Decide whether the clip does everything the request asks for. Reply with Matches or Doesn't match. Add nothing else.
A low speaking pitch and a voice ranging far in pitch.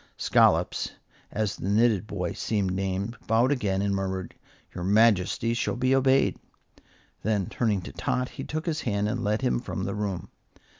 Doesn't match